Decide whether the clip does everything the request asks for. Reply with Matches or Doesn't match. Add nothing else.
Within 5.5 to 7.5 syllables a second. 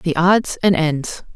Doesn't match